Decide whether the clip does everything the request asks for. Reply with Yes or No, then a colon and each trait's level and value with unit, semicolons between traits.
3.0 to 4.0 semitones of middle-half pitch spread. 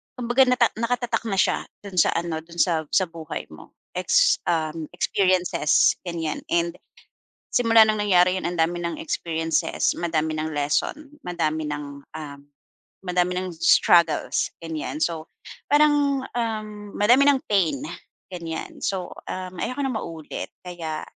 No: average, 5.2 semitones